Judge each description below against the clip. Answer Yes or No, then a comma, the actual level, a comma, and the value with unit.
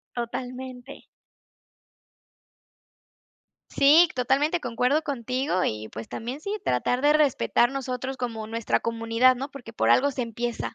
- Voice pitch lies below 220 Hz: No, very high, 250 Hz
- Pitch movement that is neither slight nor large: Yes, average, 3.1 semitones